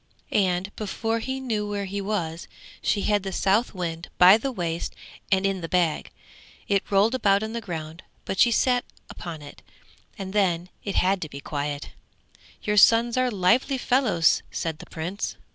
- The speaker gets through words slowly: No, average, 175 wpm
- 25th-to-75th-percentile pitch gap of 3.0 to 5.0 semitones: Yes, average, 4.1 semitones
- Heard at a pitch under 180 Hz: No, high, 195 Hz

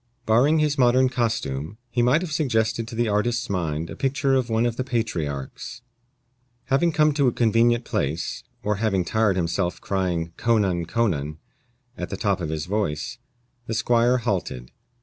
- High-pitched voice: No, low, 110 Hz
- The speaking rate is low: No, average, 170 wpm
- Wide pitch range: Yes, wide, 5.7 semitones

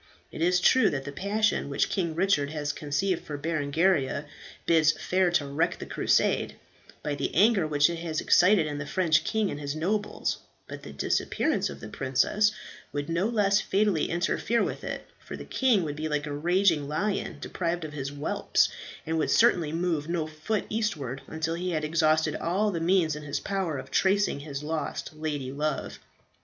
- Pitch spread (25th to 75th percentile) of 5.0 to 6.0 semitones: No, average, 4.2 semitones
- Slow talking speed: No, average, 185 wpm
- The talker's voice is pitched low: No, medium, 160 Hz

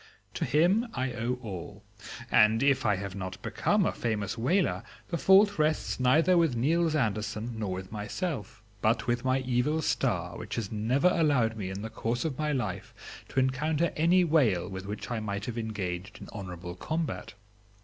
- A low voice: Yes, low, 120 Hz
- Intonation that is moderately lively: No, wide, 6.7 semitones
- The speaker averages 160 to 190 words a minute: Yes, average, 180 wpm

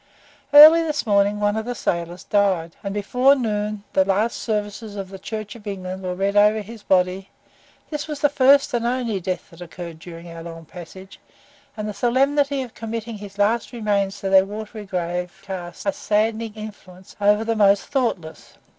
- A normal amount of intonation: Yes, average, 3.3 semitones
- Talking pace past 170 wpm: Yes, average, 180 wpm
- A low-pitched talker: No, high, 205 Hz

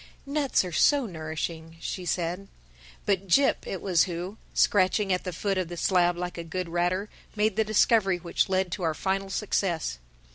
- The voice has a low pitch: No, medium, 185 Hz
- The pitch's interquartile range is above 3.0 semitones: No, narrow, 2.5 semitones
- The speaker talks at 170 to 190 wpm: Yes, average, 180 wpm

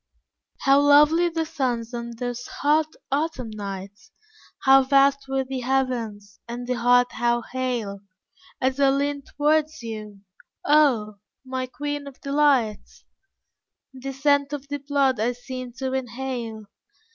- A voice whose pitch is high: Yes, very high, 260 Hz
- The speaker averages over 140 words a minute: No, slow, 135 wpm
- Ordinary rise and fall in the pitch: Yes, average, 3.0 semitones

